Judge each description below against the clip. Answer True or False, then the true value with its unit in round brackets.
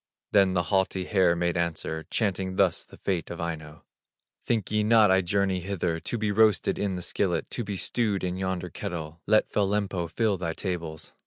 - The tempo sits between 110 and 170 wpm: False (190 wpm)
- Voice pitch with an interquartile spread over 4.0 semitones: False (2.9 semitones)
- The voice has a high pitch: False (95 Hz)